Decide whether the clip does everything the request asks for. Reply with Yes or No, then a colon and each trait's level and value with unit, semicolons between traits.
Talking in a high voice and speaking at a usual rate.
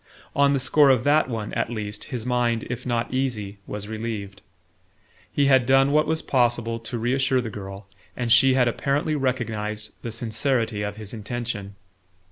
No: low, 120 Hz; average, 170 wpm